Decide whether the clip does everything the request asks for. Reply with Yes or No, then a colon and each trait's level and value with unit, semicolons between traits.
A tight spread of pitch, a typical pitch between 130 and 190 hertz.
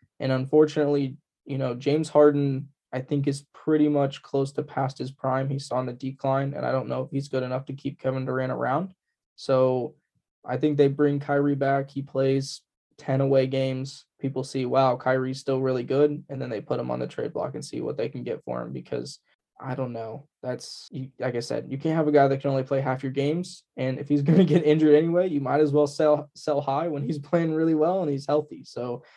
Yes: narrow, 2.1 semitones; medium, 140 Hz